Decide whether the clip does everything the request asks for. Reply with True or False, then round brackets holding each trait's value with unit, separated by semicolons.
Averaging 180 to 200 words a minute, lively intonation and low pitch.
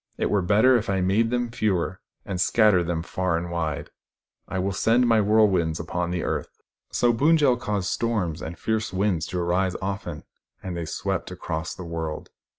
False (185 wpm; 4.0 semitones; 95 Hz)